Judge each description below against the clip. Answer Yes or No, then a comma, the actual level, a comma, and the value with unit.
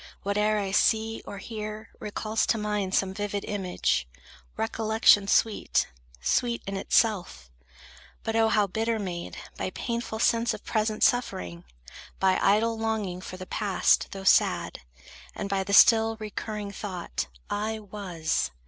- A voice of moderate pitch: No, high, 210 Hz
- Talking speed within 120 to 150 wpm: Yes, average, 140 wpm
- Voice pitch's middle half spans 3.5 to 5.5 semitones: No, narrow, 2.5 semitones